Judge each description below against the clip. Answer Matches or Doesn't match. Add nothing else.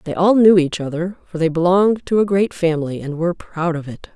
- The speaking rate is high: Matches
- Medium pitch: Matches